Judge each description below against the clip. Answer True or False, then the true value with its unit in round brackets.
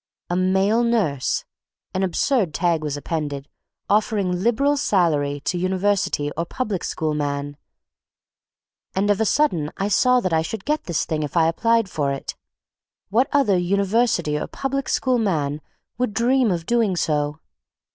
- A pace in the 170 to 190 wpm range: False (155 wpm)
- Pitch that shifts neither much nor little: False (6.6 semitones)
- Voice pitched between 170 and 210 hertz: True (185 Hz)